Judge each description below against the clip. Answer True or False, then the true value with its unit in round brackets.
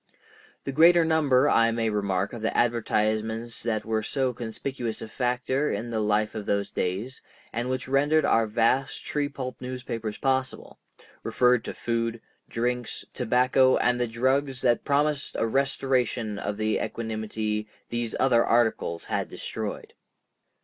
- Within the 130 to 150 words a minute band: True (145 wpm)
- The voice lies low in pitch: True (120 Hz)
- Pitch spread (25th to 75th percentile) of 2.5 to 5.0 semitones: True (3.0 semitones)